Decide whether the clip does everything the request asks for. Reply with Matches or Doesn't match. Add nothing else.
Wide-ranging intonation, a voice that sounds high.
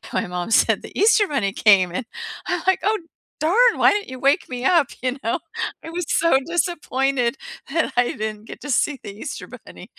Matches